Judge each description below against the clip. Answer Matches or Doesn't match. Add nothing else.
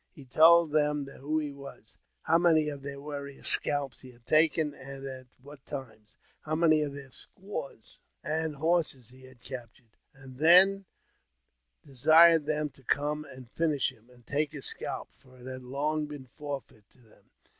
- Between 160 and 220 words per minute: Matches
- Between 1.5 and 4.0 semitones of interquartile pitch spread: Matches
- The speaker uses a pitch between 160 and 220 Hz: Doesn't match